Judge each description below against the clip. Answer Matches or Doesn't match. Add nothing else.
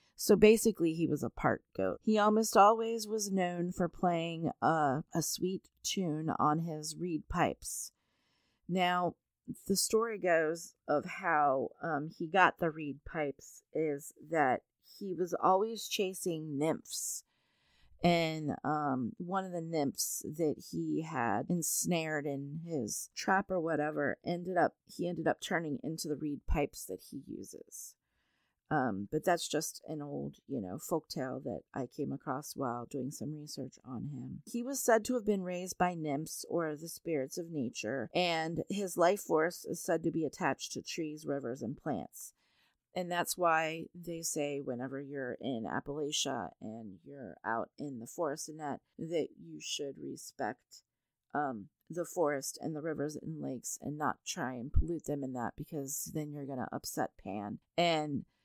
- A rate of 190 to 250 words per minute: Doesn't match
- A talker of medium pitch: Matches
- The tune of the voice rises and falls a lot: Doesn't match